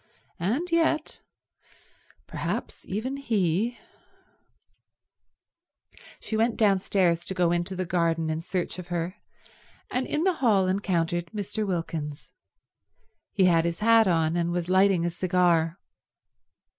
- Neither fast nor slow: No, slow, 120 wpm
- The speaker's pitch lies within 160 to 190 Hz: Yes, medium, 185 Hz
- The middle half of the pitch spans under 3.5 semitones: No, average, 4.0 semitones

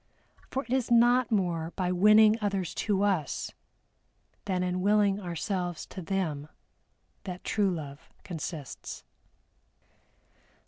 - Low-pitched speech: No, high, 190 Hz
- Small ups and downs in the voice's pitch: No, average, 3.2 semitones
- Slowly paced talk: Yes, slow, 110 wpm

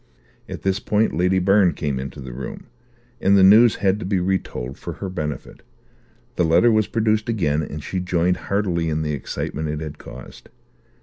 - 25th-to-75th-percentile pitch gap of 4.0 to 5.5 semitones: Yes, average, 4.5 semitones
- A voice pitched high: No, very low, 90 Hz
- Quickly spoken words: No, average, 185 wpm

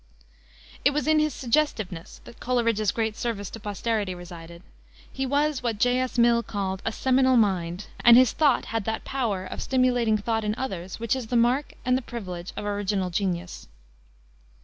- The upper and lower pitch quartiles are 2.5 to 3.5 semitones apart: No, average, 4.4 semitones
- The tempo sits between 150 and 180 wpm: Yes, average, 175 wpm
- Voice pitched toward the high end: Yes, high, 225 Hz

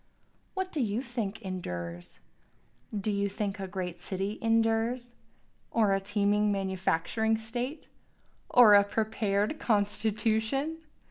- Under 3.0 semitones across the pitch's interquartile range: Yes, narrow, 2.5 semitones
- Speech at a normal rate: No, slow, 115 wpm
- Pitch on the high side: Yes, high, 210 Hz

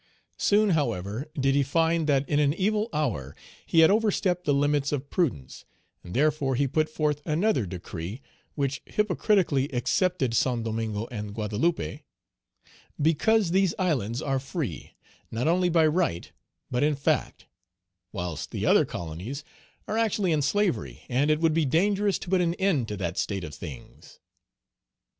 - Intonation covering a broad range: Yes, wide, 7.2 semitones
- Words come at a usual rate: Yes, average, 155 wpm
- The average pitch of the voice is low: No, medium, 145 Hz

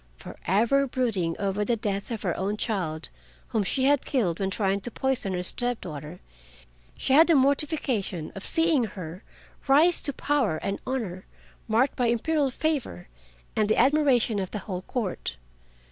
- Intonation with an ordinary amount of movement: No, wide, 5.9 semitones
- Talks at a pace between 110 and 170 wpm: Yes, average, 160 wpm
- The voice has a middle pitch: No, high, 220 Hz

